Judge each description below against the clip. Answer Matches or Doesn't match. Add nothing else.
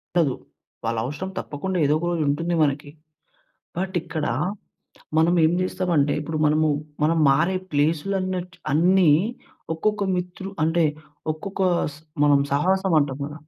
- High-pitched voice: Doesn't match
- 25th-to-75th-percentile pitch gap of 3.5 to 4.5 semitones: Matches